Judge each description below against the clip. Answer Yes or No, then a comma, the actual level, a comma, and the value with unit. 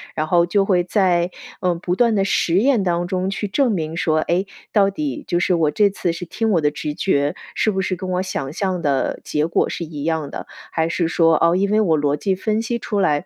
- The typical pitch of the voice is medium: Yes, medium, 180 Hz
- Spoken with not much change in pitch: No, average, 3.4 semitones